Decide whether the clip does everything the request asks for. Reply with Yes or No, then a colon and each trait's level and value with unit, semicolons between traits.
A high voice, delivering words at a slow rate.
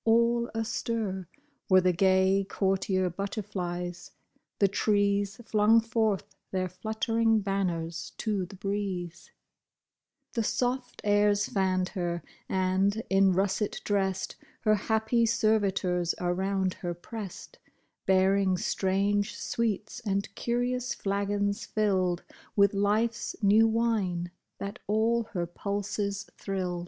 Yes: high, 200 Hz; slow, 105 wpm